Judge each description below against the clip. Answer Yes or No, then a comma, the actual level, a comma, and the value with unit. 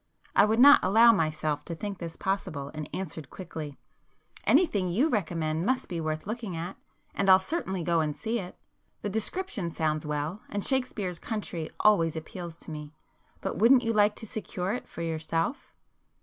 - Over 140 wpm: Yes, average, 175 wpm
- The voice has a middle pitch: Yes, medium, 180 Hz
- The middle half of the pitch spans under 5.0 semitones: No, average, 5.3 semitones